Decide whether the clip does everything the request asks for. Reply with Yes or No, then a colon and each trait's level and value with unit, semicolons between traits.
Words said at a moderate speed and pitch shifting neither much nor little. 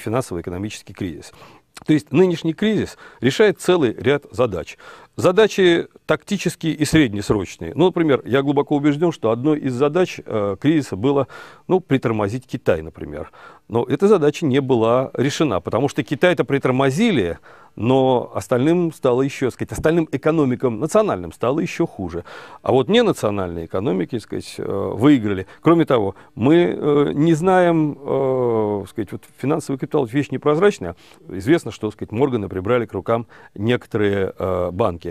No: average, 135 wpm; wide, 5.8 semitones